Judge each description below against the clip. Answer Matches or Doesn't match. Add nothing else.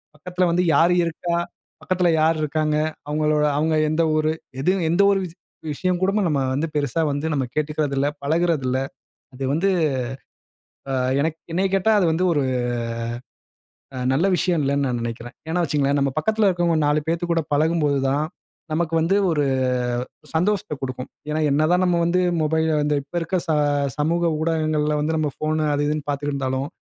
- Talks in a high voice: Doesn't match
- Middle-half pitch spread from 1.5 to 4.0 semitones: Matches